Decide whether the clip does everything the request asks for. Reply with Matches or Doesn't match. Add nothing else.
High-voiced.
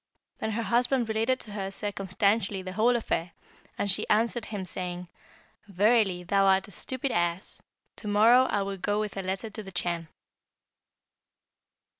Matches